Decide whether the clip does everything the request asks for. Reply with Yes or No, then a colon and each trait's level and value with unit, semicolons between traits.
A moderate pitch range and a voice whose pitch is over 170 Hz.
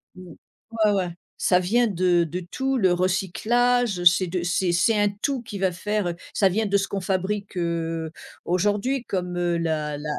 Yes: average, 3.1 semitones; medium, 185 Hz